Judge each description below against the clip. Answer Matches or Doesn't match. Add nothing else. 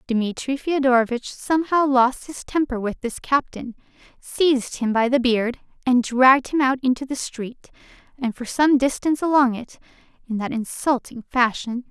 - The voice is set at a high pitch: Matches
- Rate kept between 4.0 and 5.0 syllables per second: Matches